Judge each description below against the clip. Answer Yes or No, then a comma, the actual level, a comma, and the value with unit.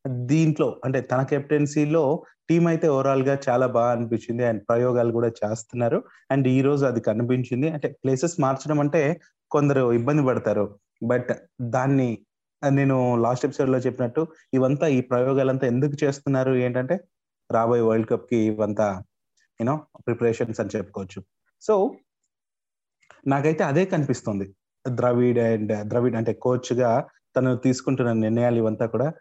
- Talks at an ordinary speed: No, fast, 130 wpm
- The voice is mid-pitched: No, low, 125 Hz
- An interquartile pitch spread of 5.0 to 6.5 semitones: No, average, 2.8 semitones